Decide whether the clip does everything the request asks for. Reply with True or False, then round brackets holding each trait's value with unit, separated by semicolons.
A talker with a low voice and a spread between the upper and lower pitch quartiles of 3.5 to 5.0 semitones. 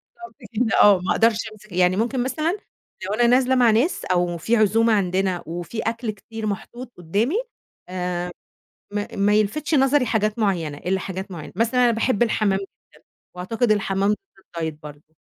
False (210 Hz; 4.2 semitones)